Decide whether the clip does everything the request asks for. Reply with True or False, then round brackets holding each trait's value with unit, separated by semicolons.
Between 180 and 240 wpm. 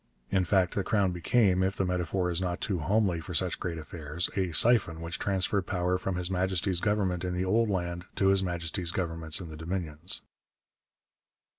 True (185 wpm)